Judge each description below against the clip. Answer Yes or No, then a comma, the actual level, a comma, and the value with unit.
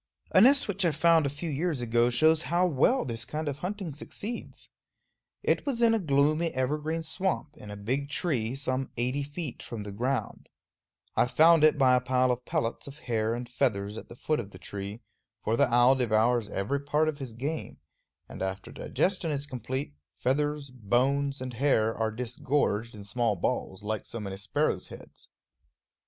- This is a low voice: Yes, low, 130 Hz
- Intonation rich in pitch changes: No, average, 4.8 semitones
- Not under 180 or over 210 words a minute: Yes, average, 185 wpm